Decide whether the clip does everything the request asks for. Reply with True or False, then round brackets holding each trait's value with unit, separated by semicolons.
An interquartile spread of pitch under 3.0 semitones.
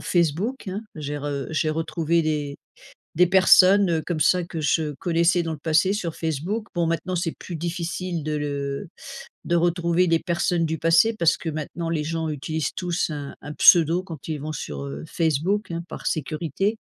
True (2.4 semitones)